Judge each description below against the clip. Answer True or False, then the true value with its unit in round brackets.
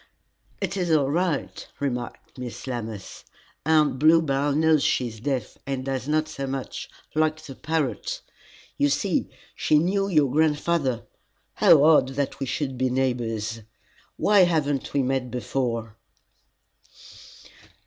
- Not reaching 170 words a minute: True (135 wpm)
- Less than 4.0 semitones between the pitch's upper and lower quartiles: True (3.6 semitones)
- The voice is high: False (140 Hz)